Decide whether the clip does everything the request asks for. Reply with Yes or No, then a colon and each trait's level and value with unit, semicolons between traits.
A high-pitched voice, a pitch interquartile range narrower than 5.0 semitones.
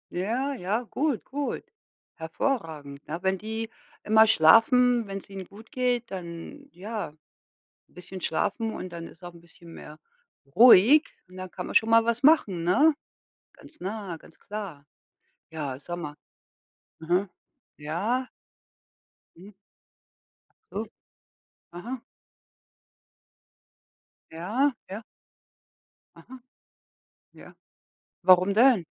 No: high, 195 Hz; average, 5.3 semitones